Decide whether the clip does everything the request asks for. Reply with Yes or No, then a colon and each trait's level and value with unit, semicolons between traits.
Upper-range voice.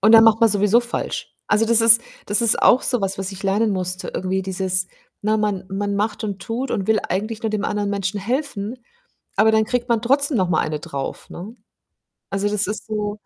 Yes: high, 210 Hz